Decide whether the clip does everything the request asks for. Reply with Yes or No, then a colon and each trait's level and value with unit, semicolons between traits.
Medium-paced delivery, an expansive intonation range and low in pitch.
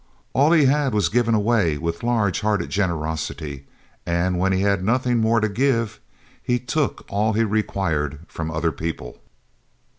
Yes: average, 155 wpm; wide, 5.8 semitones; low, 100 Hz